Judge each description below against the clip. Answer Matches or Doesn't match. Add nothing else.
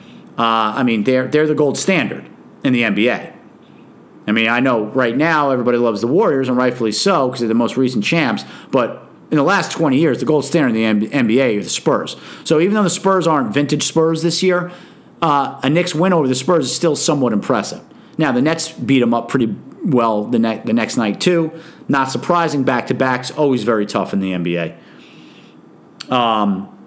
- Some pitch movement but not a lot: Doesn't match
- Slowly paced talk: Doesn't match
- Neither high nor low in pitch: Doesn't match